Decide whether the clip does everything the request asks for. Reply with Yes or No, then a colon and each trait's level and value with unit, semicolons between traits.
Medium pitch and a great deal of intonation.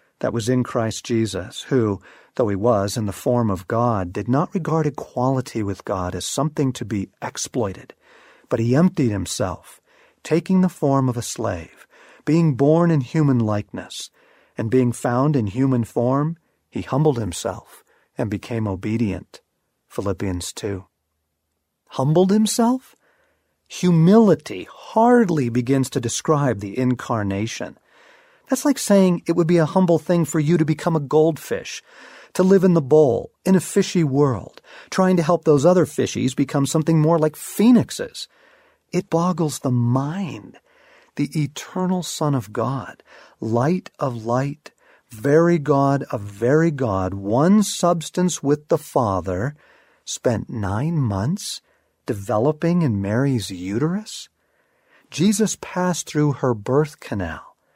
Yes: medium, 145 Hz; wide, 6.6 semitones